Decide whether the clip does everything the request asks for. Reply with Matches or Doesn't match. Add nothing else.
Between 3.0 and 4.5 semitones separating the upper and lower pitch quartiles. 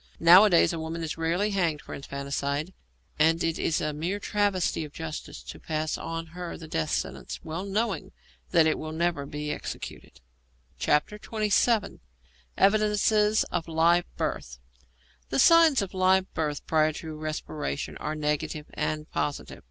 Matches